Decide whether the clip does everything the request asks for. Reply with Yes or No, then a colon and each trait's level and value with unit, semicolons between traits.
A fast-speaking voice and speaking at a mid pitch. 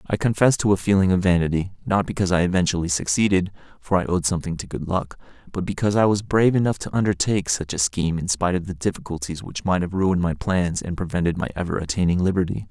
No: fast, 210 wpm; very low, 90 Hz